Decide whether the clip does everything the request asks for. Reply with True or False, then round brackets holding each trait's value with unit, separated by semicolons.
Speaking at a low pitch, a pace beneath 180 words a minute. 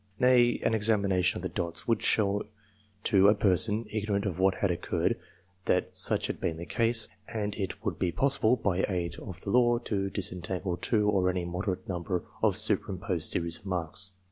False (100 Hz; 190 wpm)